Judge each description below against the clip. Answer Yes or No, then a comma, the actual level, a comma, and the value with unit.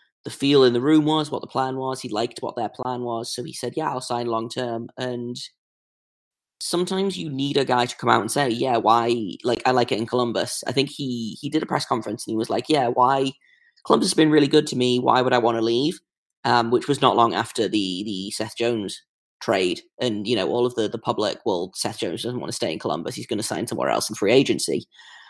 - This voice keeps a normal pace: No, fast, 250 wpm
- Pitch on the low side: Yes, low, 125 Hz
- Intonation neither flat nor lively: Yes, average, 3.6 semitones